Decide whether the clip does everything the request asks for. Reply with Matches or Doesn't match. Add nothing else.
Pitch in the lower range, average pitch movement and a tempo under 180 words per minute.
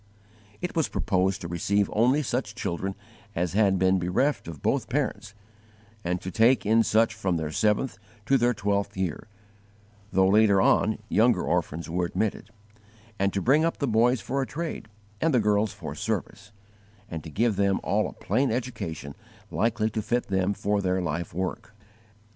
Matches